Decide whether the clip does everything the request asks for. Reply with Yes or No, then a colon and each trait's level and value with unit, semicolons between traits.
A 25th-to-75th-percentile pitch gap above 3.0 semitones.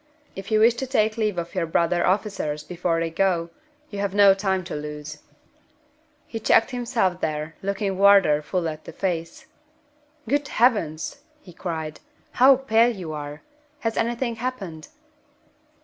Yes: average, 5.2 semitones